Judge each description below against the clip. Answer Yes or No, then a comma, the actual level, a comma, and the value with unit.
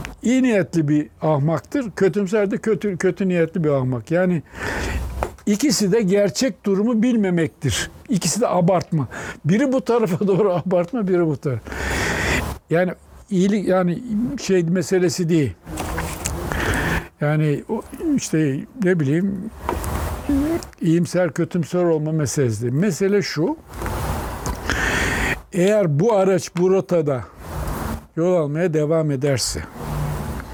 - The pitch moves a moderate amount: No, wide, 6.3 semitones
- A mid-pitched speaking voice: Yes, medium, 175 Hz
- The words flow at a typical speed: Yes, average, 105 wpm